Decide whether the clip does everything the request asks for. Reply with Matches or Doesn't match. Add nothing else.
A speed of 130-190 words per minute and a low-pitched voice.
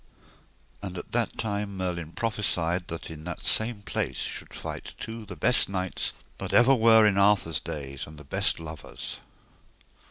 Matches